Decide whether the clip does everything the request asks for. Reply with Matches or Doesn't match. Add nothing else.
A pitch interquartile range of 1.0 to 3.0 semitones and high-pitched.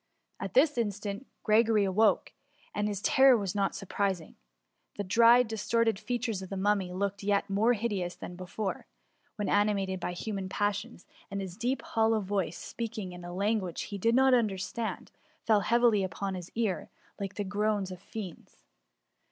Matches